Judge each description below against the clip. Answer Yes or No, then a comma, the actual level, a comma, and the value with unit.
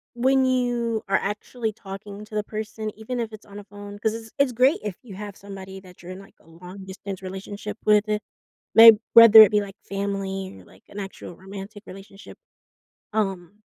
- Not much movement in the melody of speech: Yes, narrow, 2.2 semitones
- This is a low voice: No, high, 205 Hz